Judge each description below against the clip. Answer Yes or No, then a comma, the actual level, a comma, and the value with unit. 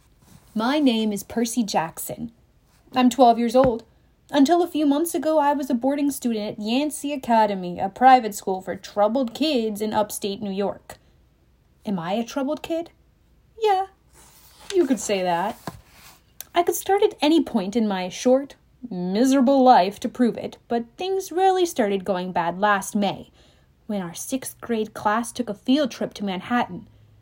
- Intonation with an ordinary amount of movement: No, wide, 5.7 semitones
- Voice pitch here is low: No, high, 235 Hz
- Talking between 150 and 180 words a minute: Yes, average, 165 wpm